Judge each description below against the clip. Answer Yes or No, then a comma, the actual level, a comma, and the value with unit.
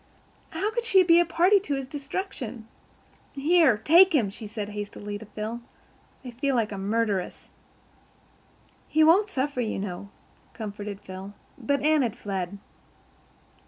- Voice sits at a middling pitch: No, high, 245 Hz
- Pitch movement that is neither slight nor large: No, wide, 7.6 semitones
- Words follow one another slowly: No, average, 145 wpm